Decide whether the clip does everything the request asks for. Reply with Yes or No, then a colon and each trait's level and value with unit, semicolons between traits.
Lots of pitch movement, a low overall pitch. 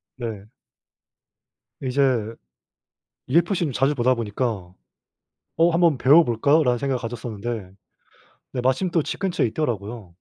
No: average, 4.8 semitones; low, 125 Hz